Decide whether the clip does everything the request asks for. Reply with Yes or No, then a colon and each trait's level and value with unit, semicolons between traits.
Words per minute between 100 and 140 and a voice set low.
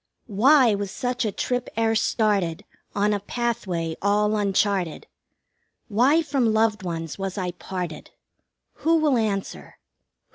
No: slow, 135 wpm; high, 210 Hz